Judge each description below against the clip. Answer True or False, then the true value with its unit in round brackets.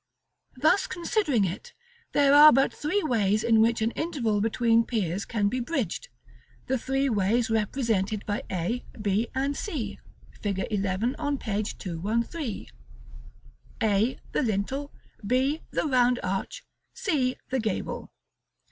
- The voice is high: True (235 Hz)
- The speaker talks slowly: True (130 wpm)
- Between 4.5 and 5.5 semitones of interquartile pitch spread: True (5.0 semitones)